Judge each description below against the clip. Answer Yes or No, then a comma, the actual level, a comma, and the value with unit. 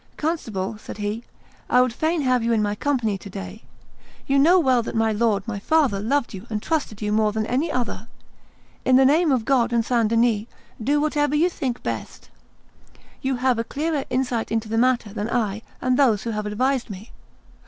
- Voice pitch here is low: No, high, 235 Hz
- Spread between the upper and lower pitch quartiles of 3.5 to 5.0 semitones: Yes, average, 4.1 semitones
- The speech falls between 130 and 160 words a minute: No, average, 200 wpm